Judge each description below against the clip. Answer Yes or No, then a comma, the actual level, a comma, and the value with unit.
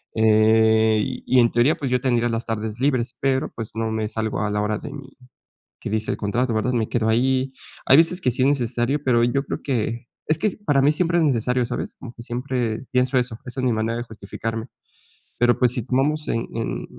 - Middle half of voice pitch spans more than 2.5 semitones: Yes, average, 2.9 semitones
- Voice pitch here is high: No, low, 120 Hz